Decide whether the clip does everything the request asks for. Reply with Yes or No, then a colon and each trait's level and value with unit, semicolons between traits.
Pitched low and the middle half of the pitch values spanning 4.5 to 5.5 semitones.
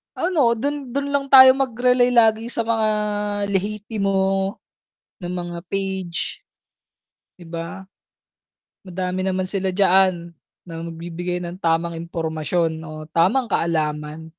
No: medium, 185 Hz; average, 5.0 semitones